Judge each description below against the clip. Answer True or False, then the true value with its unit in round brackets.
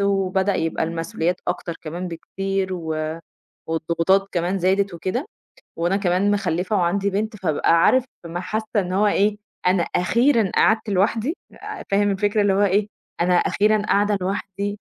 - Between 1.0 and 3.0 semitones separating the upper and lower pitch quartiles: True (2.7 semitones)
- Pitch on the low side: False (195 Hz)